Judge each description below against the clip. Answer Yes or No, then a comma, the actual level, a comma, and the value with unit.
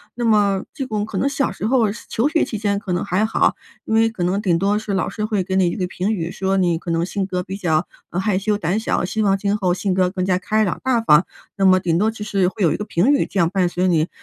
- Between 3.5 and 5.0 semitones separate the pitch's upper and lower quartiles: No, average, 2.9 semitones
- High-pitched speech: Yes, high, 195 Hz